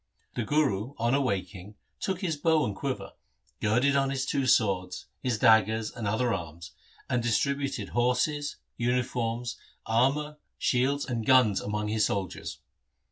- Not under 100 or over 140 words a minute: Yes, slow, 135 wpm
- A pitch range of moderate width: Yes, average, 4.5 semitones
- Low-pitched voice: Yes, low, 120 Hz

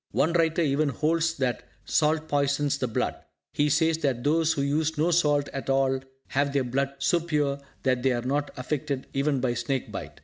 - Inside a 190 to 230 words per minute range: Yes, average, 195 wpm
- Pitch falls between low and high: Yes, medium, 145 Hz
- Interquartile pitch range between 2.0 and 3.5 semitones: Yes, narrow, 2.5 semitones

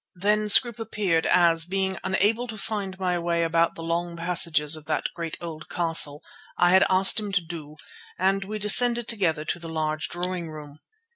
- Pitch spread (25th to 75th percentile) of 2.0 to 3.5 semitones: Yes, average, 3.2 semitones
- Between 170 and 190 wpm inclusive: Yes, average, 185 wpm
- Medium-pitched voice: Yes, medium, 175 Hz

